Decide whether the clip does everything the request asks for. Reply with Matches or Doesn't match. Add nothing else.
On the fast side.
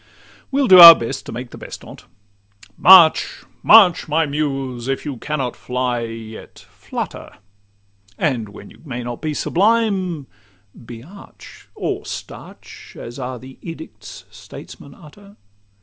Doesn't match